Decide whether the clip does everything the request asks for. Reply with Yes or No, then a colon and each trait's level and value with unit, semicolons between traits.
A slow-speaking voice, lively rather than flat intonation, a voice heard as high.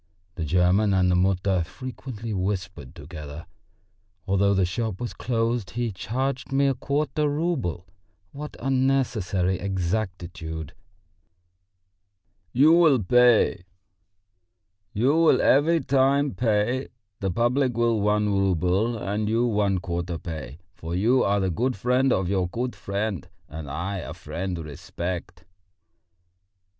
No: slow, 115 wpm; wide, 5.7 semitones; low, 100 Hz